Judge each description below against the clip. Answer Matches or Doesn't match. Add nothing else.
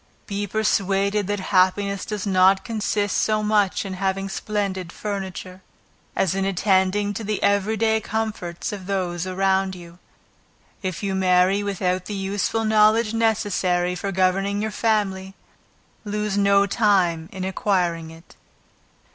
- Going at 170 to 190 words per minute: Doesn't match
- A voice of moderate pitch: Doesn't match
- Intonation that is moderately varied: Doesn't match